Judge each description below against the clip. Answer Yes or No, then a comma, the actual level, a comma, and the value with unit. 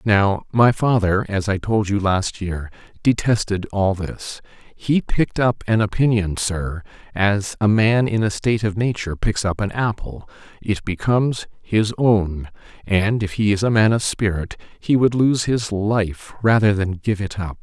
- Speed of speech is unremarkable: Yes, average, 165 wpm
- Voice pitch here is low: Yes, low, 105 Hz